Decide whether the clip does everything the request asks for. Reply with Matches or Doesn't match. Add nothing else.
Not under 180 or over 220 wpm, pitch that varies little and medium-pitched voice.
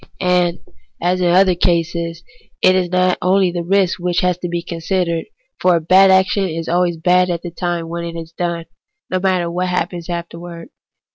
Matches